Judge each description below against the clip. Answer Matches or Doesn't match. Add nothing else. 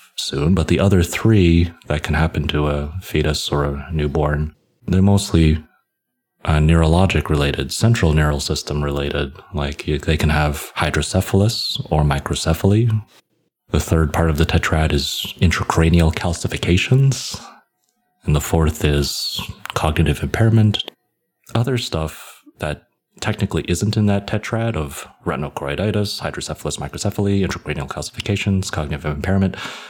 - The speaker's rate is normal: Doesn't match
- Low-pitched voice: Matches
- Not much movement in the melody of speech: Doesn't match